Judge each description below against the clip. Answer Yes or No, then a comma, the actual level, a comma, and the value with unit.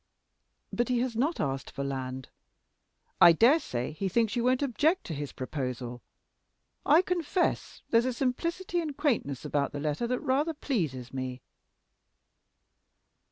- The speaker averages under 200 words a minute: Yes, average, 145 wpm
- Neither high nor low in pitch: No, high, 230 Hz